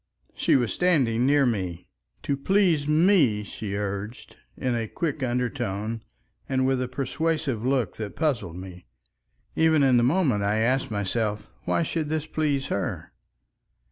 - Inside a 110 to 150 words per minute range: Yes, average, 145 wpm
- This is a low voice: Yes, low, 125 Hz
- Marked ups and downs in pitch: Yes, wide, 5.9 semitones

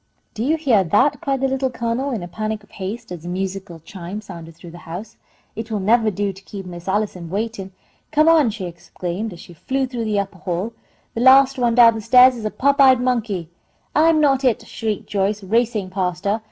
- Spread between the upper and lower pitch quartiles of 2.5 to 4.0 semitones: No, average, 4.9 semitones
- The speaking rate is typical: No, fast, 220 wpm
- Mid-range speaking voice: No, high, 215 Hz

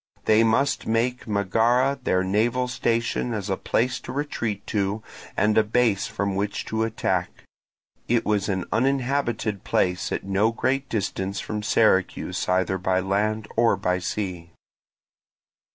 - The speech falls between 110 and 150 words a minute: Yes, average, 140 wpm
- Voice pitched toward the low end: Yes, low, 110 Hz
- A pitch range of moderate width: Yes, average, 3.3 semitones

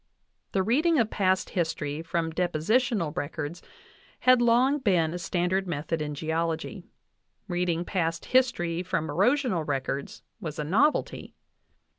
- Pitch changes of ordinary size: Yes, average, 4.9 semitones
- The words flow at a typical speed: No, slow, 130 wpm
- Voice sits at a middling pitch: Yes, medium, 175 Hz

